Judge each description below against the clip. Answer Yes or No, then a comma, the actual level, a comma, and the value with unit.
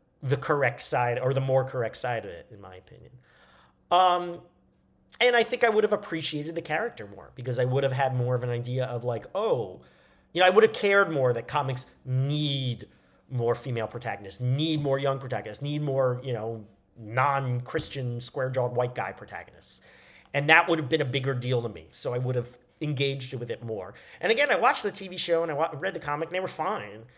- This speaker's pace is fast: Yes, fast, 215 wpm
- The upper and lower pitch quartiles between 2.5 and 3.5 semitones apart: No, average, 4.3 semitones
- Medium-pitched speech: No, low, 130 Hz